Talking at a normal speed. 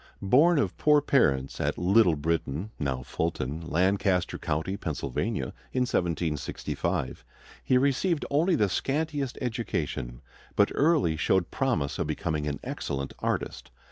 No: slow, 125 wpm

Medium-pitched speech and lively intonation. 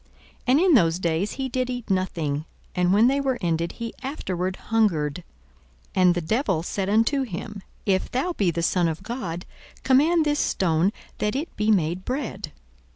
No: high, 200 Hz; wide, 6.7 semitones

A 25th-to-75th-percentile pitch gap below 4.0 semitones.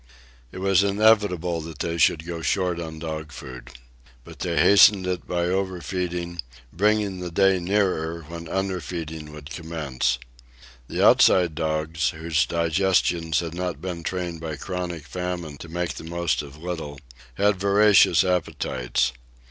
Yes: narrow, 2.5 semitones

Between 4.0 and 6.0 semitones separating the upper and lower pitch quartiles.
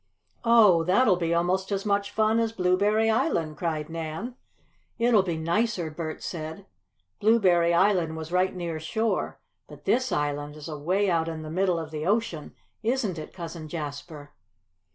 Yes: average, 4.5 semitones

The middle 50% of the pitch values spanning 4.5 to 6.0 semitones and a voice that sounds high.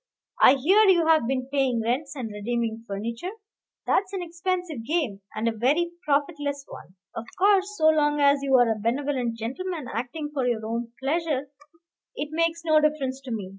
Yes: wide, 5.5 semitones; very high, 280 Hz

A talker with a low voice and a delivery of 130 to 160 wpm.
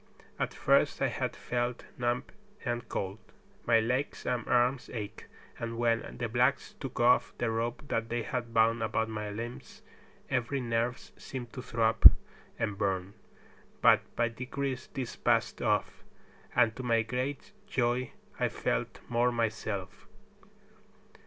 Yes: low, 120 Hz; average, 140 wpm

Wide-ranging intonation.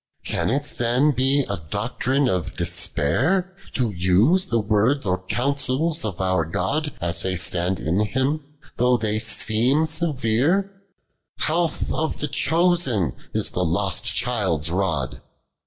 Yes: wide, 7.8 semitones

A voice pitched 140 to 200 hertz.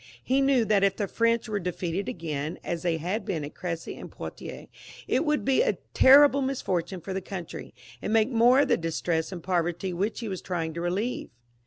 Yes: high, 190 Hz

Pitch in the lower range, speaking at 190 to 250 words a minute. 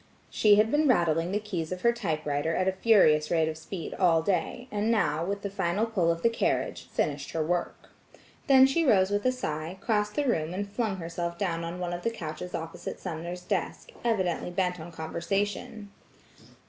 No: medium, 180 Hz; average, 195 wpm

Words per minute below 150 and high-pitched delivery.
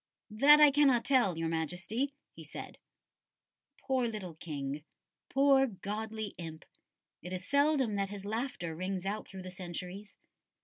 Yes: average, 140 wpm; high, 205 Hz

